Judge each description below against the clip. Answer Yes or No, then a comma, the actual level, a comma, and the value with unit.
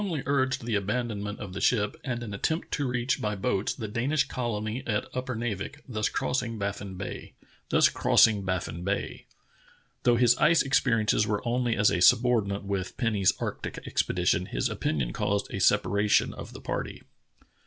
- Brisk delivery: No, average, 155 wpm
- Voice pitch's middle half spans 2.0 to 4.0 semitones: Yes, average, 3.6 semitones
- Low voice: Yes, low, 110 Hz